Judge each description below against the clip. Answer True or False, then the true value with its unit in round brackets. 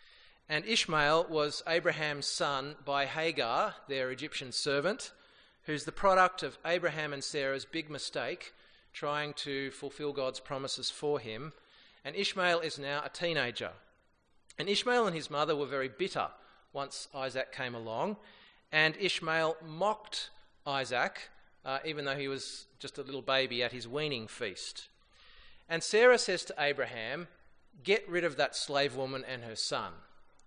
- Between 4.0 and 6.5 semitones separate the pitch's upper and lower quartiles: False (3.4 semitones)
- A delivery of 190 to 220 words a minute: False (150 wpm)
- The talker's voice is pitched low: False (145 Hz)